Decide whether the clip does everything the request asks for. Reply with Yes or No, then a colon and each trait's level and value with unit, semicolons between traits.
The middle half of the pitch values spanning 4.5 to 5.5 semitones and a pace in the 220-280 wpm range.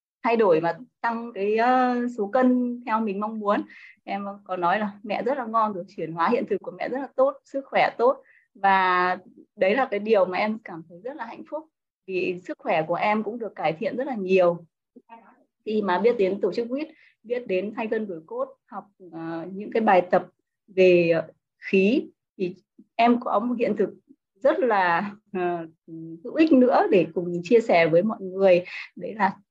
No: average, 5.1 semitones; average, 195 wpm